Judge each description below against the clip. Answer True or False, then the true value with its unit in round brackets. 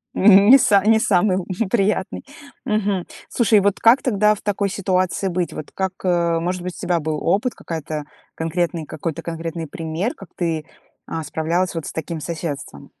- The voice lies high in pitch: False (180 Hz)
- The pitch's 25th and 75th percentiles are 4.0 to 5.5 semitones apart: False (3.4 semitones)